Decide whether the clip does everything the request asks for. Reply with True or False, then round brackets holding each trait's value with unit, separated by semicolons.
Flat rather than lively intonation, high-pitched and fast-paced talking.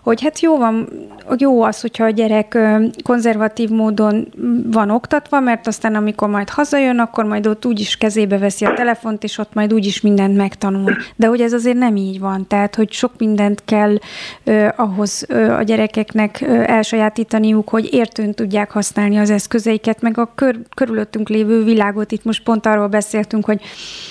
True (1.7 semitones; 220 Hz; 175 wpm)